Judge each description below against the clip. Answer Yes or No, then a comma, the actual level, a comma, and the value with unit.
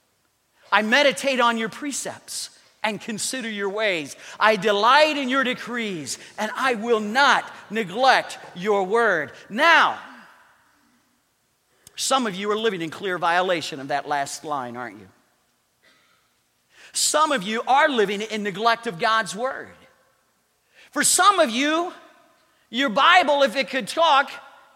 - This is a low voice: No, high, 235 Hz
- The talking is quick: No, slow, 135 wpm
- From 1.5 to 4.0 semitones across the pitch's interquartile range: No, average, 5.1 semitones